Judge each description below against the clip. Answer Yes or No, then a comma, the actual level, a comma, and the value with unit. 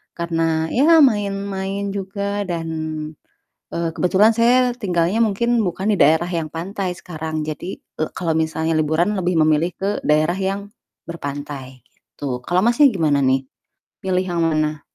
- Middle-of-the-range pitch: Yes, medium, 175 Hz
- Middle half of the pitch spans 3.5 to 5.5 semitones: Yes, average, 4.1 semitones